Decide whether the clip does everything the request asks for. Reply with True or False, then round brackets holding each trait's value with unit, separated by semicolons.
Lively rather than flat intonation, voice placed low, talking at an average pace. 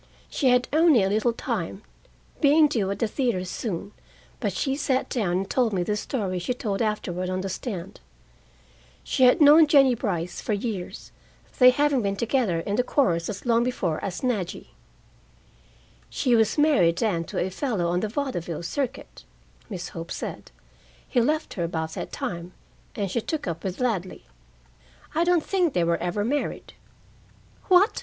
False (6.4 semitones; 215 Hz; 170 wpm)